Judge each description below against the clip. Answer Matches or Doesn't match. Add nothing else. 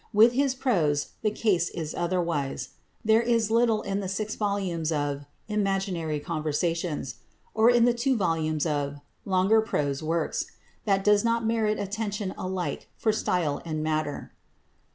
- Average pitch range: Doesn't match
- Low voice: Doesn't match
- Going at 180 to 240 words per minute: Doesn't match